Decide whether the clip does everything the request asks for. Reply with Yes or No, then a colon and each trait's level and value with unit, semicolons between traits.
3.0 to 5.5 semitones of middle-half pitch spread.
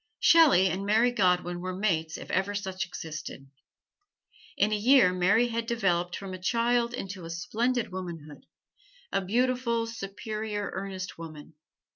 Yes: average, 4.3 semitones